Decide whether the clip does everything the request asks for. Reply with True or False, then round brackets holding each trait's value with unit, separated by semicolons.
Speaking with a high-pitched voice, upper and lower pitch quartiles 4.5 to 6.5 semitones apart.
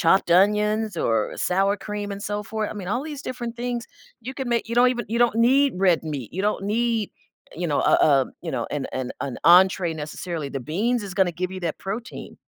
True (200 Hz; 5.4 semitones)